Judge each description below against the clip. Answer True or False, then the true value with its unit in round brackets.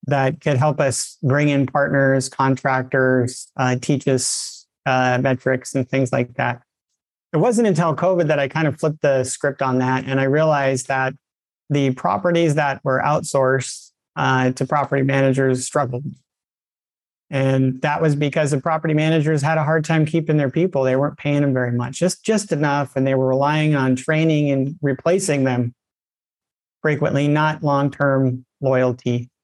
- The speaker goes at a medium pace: True (165 wpm)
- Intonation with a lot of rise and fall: False (2.6 semitones)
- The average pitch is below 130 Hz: False (140 Hz)